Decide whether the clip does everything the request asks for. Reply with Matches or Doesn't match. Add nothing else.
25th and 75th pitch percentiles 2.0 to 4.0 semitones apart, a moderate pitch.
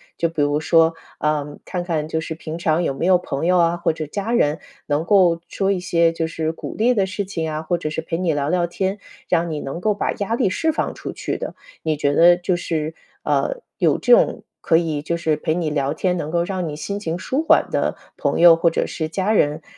Matches